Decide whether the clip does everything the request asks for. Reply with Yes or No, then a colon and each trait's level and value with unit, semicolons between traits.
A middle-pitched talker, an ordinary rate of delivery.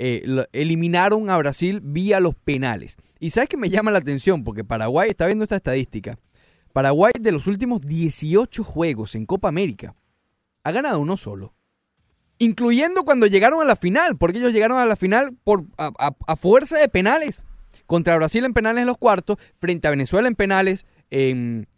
Yes: medium, 175 Hz; average, 180 wpm